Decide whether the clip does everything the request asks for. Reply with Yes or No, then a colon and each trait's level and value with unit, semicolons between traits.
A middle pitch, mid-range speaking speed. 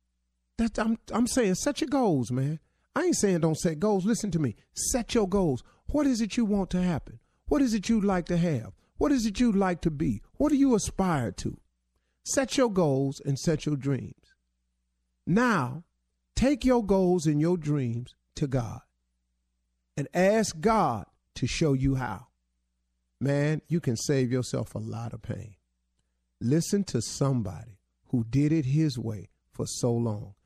Yes: medium, 145 Hz; average, 175 wpm